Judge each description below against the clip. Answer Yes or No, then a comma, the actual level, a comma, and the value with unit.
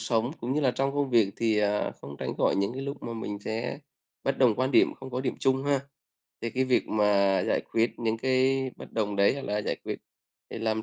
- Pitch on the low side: Yes, low, 115 Hz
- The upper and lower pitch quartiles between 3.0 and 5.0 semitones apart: Yes, average, 3.9 semitones